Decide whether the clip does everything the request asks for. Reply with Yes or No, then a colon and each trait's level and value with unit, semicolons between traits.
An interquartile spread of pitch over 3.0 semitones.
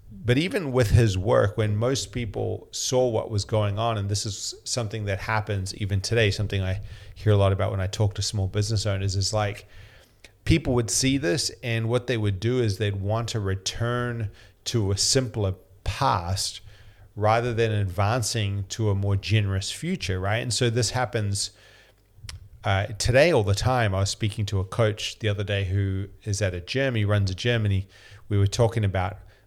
No: narrow, 2.6 semitones